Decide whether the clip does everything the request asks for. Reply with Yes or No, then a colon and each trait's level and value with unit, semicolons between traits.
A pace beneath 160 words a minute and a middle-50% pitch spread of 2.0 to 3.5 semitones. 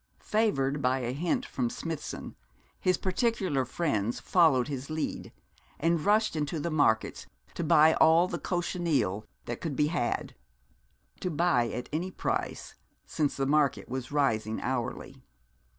No: average, 140 wpm; average, 5.0 semitones